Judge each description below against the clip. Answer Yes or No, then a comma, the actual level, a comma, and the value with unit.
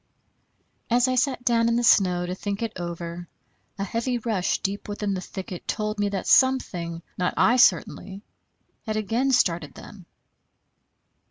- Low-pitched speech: No, high, 205 Hz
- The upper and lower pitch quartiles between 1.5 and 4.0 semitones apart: No, average, 4.6 semitones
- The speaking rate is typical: Yes, average, 155 wpm